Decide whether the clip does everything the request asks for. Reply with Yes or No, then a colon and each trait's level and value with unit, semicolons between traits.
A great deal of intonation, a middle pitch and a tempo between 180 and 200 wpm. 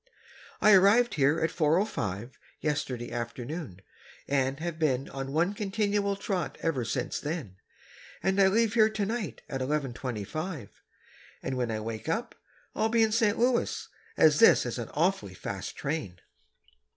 No: wide, 8.0 semitones; medium, 155 Hz; average, 145 wpm